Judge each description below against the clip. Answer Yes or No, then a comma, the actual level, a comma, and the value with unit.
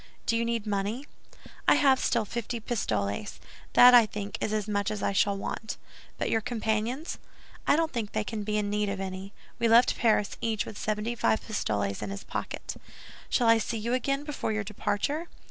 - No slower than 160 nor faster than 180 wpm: No, average, 195 wpm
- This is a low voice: No, high, 215 Hz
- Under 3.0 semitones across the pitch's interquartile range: Yes, narrow, 2.6 semitones